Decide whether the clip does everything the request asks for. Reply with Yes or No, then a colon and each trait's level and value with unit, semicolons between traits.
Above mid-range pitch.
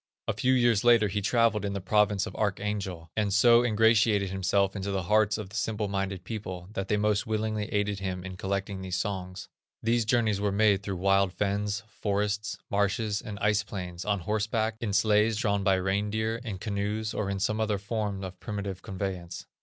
No: low, 100 Hz